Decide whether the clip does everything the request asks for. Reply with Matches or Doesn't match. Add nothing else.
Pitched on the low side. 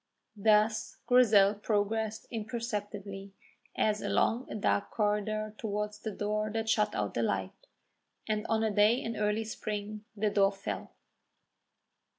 Doesn't match